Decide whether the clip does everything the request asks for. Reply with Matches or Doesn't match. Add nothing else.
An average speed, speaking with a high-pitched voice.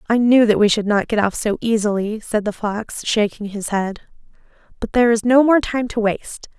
Doesn't match